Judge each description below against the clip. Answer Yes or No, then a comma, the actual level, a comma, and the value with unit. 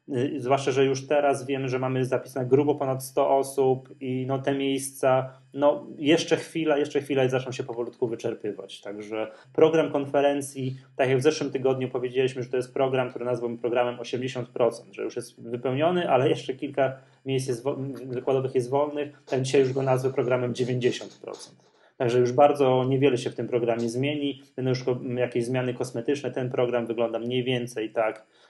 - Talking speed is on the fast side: Yes, fast, 175 wpm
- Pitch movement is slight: Yes, narrow, 1.8 semitones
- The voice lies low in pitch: Yes, low, 130 Hz